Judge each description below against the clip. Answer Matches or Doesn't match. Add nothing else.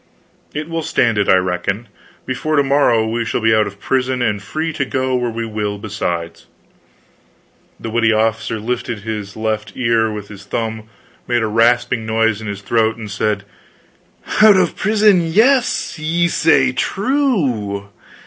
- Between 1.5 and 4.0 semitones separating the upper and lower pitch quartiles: Doesn't match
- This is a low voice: Matches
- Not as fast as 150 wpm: Doesn't match